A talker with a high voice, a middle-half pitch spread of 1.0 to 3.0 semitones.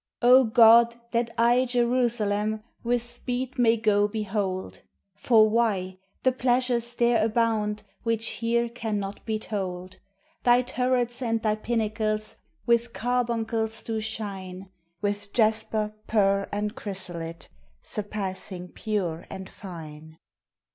Yes: high, 220 Hz; average, 2.7 semitones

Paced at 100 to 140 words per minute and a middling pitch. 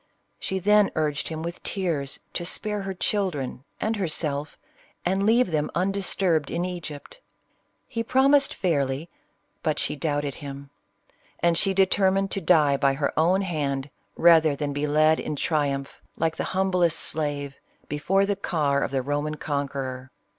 No: average, 160 wpm; medium, 160 Hz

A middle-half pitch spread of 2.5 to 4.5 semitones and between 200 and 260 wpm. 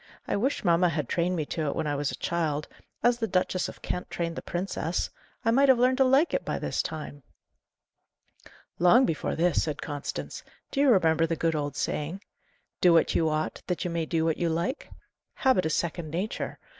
Yes: average, 3.7 semitones; fast, 205 wpm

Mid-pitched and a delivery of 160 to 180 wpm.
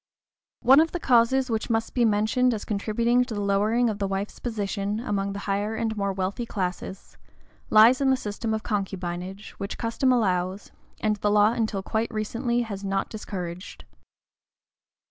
No: high, 215 Hz; average, 165 wpm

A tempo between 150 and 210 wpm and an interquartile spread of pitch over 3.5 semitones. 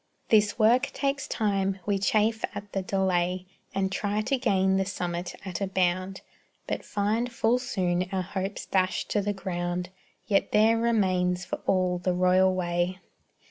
No: average, 160 wpm; narrow, 2.5 semitones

